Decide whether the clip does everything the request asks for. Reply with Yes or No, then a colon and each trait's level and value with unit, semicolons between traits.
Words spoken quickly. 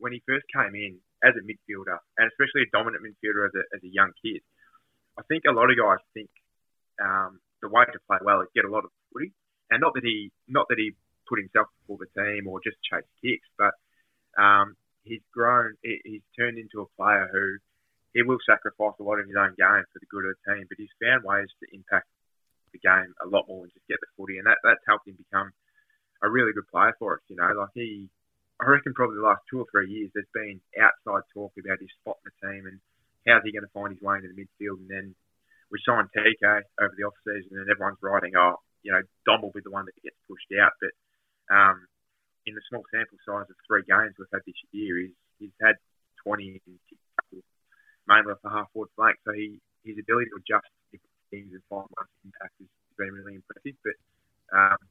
Yes: fast, 230 wpm